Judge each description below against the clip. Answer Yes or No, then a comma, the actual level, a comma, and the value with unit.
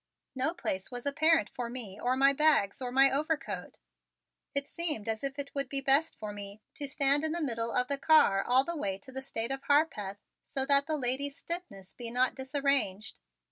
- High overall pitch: Yes, very high, 270 Hz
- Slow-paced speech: No, fast, 205 wpm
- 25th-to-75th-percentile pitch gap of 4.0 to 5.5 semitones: No, average, 3.5 semitones